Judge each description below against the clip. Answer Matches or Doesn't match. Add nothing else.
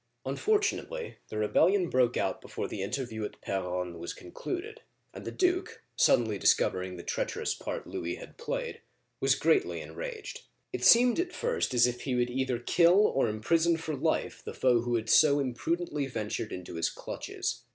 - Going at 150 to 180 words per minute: Matches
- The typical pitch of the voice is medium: Doesn't match